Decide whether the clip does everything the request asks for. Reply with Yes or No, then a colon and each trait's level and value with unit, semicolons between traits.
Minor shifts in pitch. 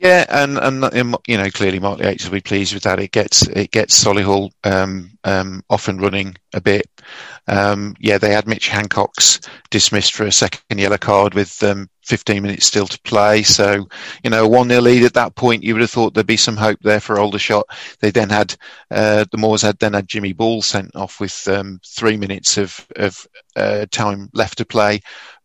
Yes: narrow, 1.8 semitones